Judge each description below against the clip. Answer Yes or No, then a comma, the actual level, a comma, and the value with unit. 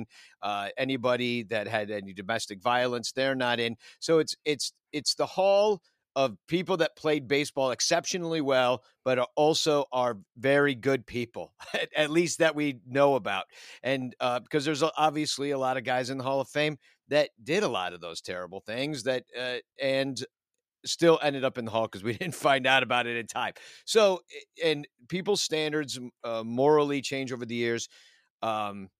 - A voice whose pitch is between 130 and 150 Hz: Yes, low, 135 Hz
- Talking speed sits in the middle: Yes, average, 180 wpm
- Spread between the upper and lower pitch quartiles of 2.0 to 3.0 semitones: No, average, 3.8 semitones